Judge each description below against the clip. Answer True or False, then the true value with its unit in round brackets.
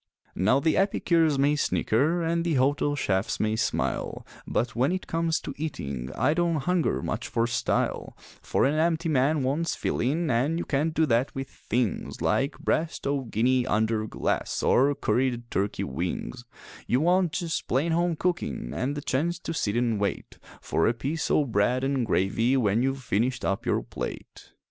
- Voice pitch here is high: False (135 Hz)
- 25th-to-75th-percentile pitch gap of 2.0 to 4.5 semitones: False (5.5 semitones)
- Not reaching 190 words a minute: True (175 wpm)